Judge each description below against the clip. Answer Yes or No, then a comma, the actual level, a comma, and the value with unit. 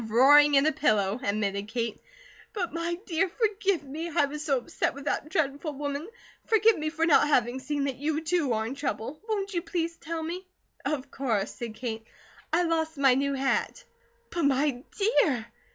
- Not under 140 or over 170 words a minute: No, average, 185 wpm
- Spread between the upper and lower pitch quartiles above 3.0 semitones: Yes, average, 4.4 semitones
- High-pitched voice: Yes, very high, 290 Hz